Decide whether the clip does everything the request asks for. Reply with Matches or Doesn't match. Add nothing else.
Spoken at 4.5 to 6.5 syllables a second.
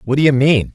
Matches